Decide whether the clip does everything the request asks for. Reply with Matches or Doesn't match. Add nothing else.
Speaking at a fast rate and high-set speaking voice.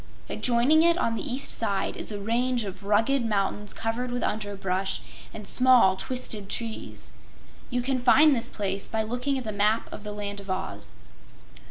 Doesn't match